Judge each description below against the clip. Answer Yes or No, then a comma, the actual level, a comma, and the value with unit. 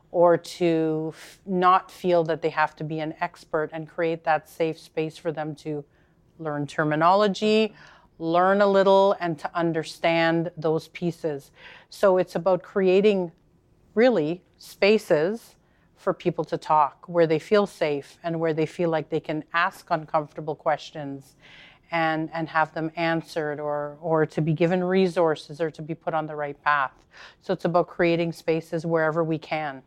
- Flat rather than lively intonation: Yes, narrow, 2.0 semitones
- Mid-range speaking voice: Yes, medium, 165 Hz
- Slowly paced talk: No, average, 165 wpm